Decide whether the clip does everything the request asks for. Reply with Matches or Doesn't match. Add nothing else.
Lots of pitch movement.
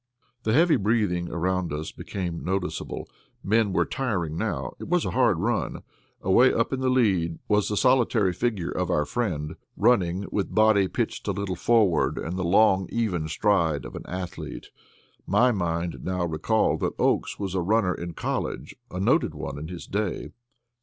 Doesn't match